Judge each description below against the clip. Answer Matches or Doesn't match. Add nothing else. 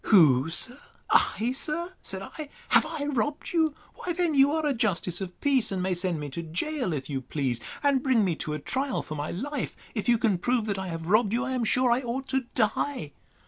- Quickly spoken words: Matches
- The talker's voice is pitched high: Matches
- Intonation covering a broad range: Matches